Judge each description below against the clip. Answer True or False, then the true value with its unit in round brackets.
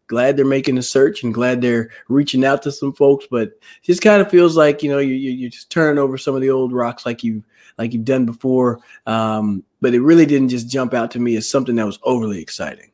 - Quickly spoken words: True (255 wpm)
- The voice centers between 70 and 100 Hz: False (130 Hz)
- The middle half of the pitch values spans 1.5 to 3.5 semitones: True (2.9 semitones)